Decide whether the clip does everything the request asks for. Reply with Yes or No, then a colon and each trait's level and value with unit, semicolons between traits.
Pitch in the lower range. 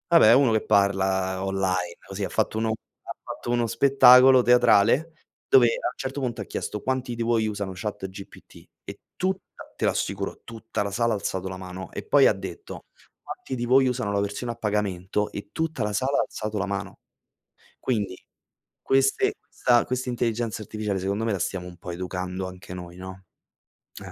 Yes: low, 105 Hz